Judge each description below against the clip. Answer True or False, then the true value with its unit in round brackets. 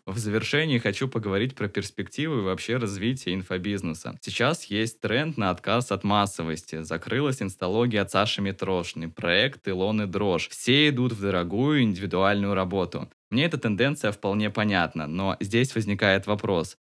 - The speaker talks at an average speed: True (145 wpm)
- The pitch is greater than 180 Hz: False (100 Hz)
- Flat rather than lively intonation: False (3.4 semitones)